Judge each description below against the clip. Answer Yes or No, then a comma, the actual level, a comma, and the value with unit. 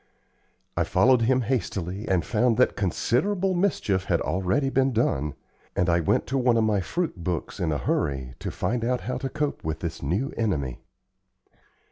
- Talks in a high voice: No, low, 110 Hz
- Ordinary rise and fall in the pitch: No, wide, 7.0 semitones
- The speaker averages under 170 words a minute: No, average, 175 wpm